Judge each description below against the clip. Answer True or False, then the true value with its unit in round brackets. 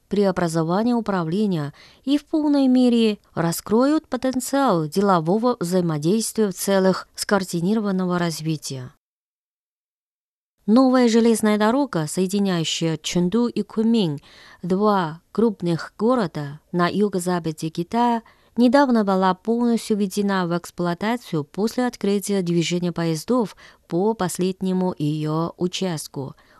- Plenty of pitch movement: False (4.8 semitones)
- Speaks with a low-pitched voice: False (195 Hz)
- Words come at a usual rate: False (95 wpm)